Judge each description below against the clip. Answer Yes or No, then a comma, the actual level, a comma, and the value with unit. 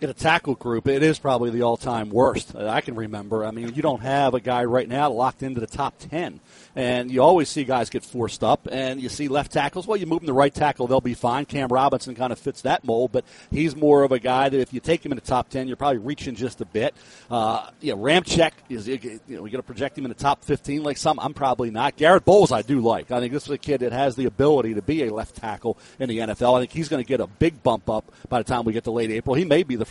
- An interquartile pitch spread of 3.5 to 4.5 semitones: No, average, 2.8 semitones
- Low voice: Yes, low, 130 Hz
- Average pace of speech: No, fast, 285 wpm